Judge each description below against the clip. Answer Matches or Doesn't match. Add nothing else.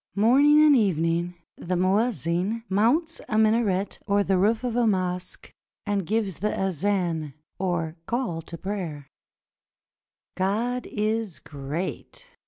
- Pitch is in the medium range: Doesn't match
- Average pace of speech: Doesn't match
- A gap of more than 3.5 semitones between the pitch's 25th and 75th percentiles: Matches